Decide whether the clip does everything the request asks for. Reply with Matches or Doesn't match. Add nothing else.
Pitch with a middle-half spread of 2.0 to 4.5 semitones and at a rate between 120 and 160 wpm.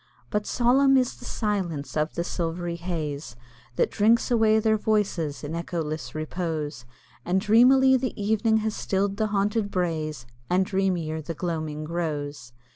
Doesn't match